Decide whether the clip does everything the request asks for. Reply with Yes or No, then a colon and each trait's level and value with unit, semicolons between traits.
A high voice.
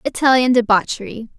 Yes: high, 240 Hz